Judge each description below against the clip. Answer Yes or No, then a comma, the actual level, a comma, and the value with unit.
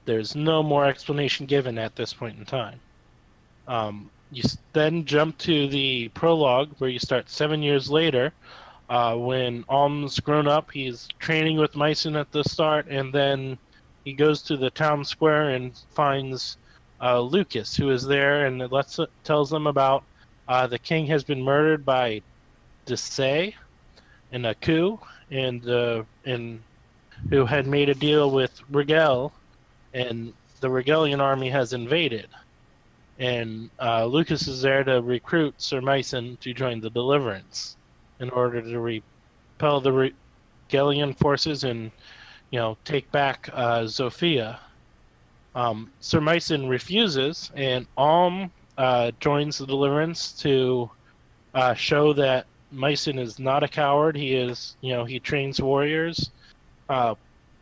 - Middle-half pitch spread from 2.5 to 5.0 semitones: Yes, average, 3.4 semitones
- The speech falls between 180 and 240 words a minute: No, average, 145 wpm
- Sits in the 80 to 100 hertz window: No, low, 135 Hz